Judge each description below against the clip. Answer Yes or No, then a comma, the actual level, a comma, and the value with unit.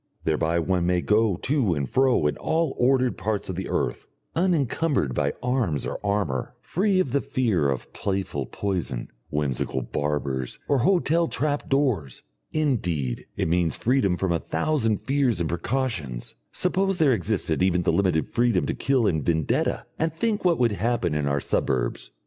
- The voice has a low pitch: Yes, low, 100 Hz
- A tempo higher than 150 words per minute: Yes, average, 165 wpm